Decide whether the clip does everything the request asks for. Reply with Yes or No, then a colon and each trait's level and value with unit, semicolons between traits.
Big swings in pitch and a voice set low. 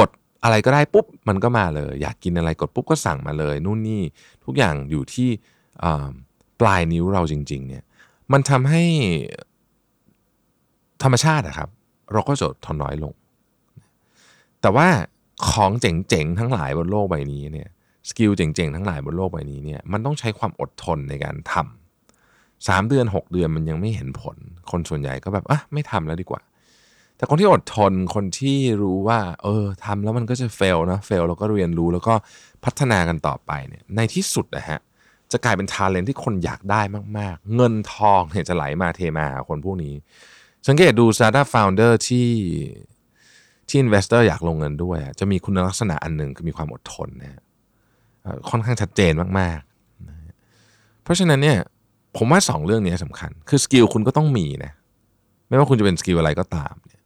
Yes: wide, 5.9 semitones; low, 100 Hz